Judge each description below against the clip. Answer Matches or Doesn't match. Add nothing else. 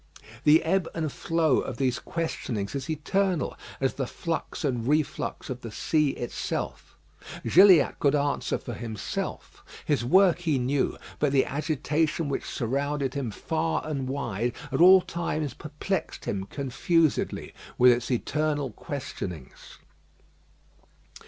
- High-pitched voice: Doesn't match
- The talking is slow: Matches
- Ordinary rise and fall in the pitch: Matches